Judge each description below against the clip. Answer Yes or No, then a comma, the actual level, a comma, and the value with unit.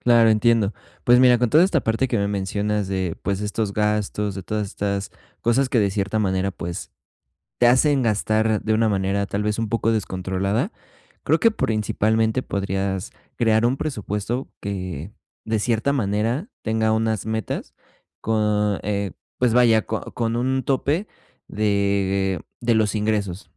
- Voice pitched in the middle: No, low, 110 Hz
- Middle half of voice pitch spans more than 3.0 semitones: No, average, 2.7 semitones